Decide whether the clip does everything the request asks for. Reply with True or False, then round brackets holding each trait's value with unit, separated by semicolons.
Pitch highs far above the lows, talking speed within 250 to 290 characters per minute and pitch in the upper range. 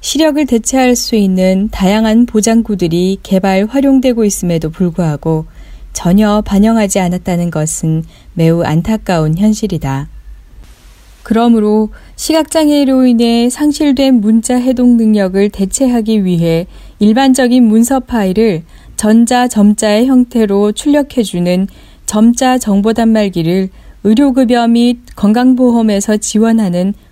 False (4.4 semitones; 275 characters per minute; 215 Hz)